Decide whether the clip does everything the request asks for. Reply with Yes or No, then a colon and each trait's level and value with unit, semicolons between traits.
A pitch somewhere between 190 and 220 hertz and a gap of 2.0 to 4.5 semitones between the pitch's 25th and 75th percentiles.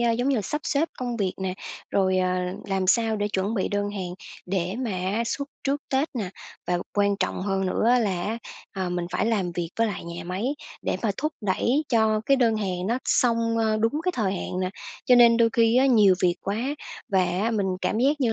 Yes: high, 210 Hz; average, 3.9 semitones